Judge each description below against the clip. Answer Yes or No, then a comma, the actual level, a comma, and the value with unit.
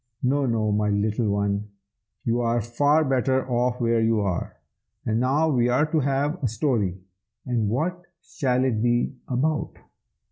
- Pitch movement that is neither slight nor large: Yes, average, 3.8 semitones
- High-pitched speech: No, low, 120 Hz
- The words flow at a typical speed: Yes, average, 155 wpm